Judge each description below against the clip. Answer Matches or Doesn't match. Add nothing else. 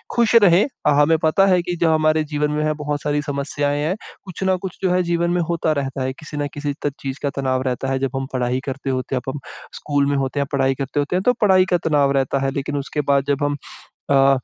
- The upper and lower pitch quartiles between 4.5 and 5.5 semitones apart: Doesn't match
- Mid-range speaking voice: Matches